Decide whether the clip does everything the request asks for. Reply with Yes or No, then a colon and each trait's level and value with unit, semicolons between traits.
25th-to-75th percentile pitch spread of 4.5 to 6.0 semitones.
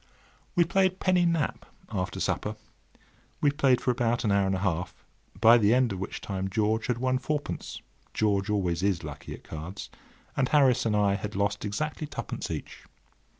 Yes: average, 5.2 semitones